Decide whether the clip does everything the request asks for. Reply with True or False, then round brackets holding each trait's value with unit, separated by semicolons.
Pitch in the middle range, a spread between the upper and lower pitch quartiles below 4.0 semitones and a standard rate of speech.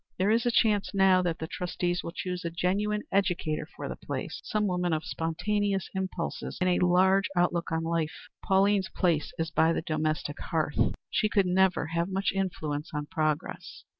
True (180 Hz; 2.9 semitones; 180 wpm)